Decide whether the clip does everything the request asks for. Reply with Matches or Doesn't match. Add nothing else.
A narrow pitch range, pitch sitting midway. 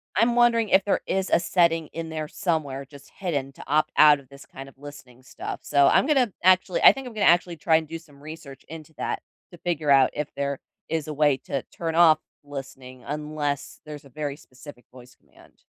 Doesn't match